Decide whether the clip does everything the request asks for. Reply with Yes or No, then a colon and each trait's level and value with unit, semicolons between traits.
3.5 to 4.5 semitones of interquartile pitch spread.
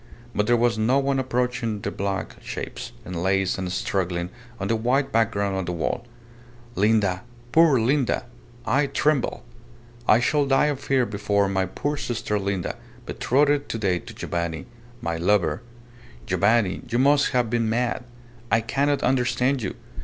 No: average, 5.2 semitones